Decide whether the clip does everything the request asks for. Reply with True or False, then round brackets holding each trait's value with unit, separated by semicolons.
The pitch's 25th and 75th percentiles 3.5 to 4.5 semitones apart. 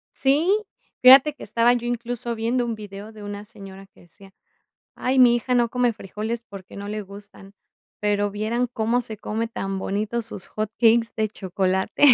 False (2.8 semitones)